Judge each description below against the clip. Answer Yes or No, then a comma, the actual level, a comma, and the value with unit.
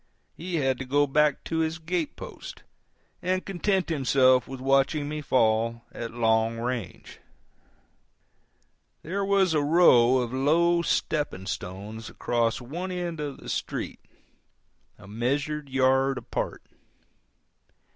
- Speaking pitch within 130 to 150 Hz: Yes, low, 135 Hz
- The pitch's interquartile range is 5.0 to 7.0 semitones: Yes, average, 5.3 semitones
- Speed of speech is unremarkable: No, slow, 125 wpm